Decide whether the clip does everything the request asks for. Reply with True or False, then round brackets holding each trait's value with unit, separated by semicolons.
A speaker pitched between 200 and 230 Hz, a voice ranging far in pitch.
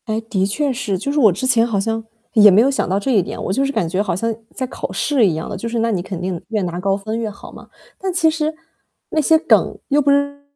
True (225 Hz; 6.0 semitones)